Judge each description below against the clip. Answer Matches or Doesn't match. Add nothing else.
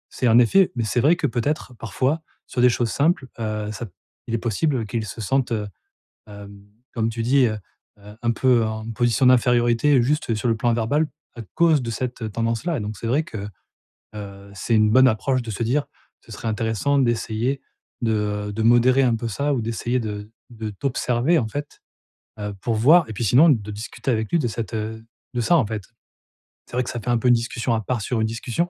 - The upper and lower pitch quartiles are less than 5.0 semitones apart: Matches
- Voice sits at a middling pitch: Doesn't match